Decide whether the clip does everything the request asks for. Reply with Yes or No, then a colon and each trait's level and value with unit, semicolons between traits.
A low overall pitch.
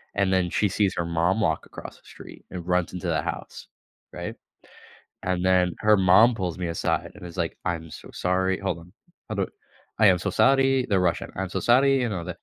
Yes: very low, 95 Hz